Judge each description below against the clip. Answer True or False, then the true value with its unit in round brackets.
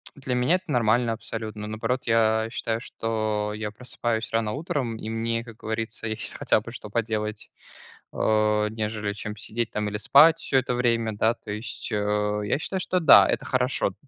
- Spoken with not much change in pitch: True (2.2 semitones)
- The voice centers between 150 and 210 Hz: False (110 Hz)